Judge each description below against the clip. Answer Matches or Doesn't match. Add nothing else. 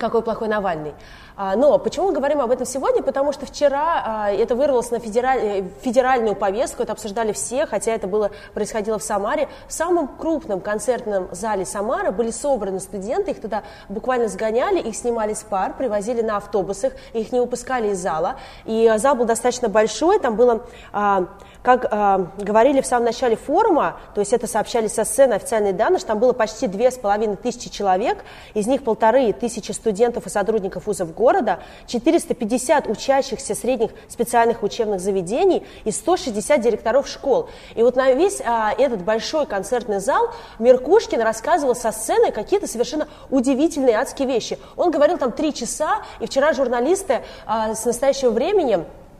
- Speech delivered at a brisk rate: Matches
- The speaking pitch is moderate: Doesn't match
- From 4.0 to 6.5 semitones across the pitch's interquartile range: Matches